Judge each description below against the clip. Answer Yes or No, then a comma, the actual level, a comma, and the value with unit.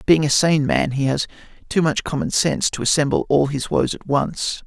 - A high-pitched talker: No, medium, 145 Hz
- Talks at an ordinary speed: No, fast, 220 wpm